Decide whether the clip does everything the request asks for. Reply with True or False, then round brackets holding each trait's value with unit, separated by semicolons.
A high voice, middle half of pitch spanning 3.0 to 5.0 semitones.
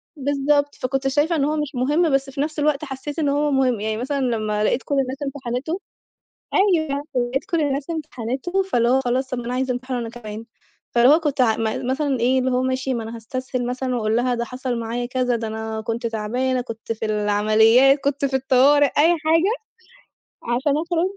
True (260 Hz; 3.3 semitones)